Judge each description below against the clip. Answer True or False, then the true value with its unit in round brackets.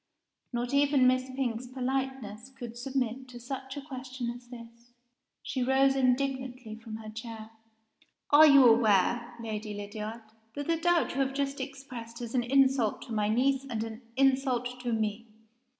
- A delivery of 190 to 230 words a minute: False (160 wpm)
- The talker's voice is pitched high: True (250 Hz)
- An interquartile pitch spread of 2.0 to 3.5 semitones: True (2.7 semitones)